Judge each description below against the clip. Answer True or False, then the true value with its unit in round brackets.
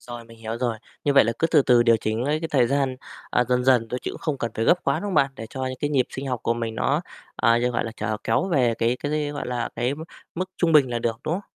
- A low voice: True (125 Hz)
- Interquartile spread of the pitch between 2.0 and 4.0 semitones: True (3.7 semitones)